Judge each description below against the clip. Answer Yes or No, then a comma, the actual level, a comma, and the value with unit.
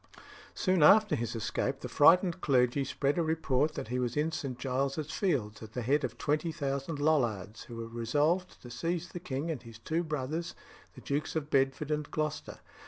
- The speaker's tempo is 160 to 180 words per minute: No, average, 190 wpm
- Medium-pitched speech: Yes, medium, 145 Hz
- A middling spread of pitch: Yes, average, 4.3 semitones